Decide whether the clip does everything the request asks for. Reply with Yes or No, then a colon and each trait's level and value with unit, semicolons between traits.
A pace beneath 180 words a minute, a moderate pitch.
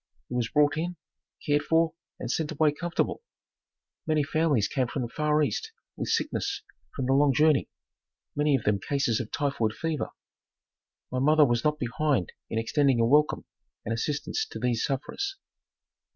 Yes: average, 165 wpm; medium, 145 Hz